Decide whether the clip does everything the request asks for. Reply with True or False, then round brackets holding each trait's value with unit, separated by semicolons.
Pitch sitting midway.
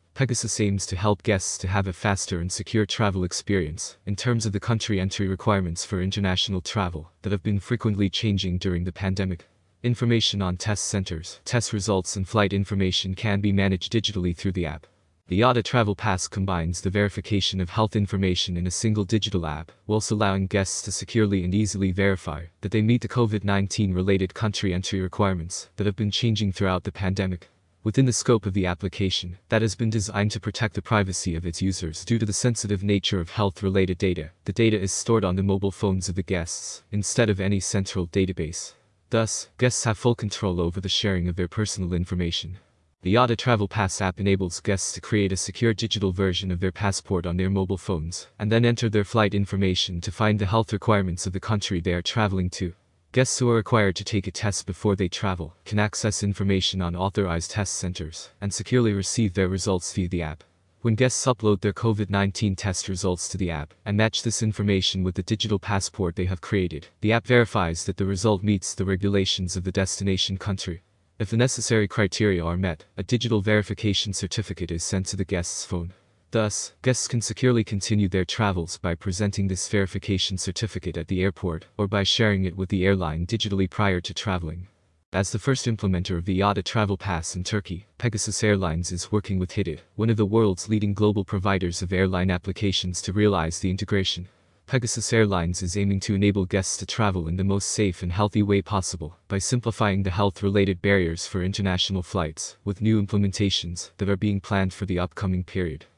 False (100 Hz)